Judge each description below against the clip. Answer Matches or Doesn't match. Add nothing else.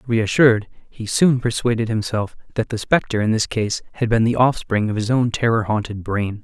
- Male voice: Matches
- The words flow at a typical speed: Matches